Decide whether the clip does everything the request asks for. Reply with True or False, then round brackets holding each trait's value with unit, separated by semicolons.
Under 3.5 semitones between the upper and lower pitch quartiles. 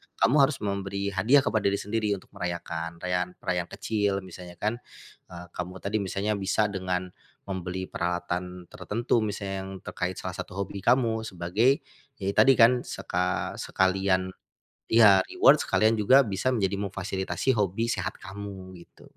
True (2.8 semitones)